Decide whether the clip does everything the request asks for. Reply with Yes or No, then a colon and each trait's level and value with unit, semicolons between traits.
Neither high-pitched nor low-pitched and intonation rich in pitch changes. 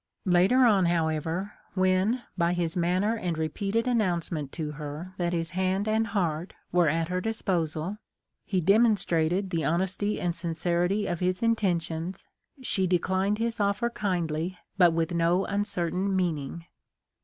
No: medium, 180 Hz; average, 3.1 semitones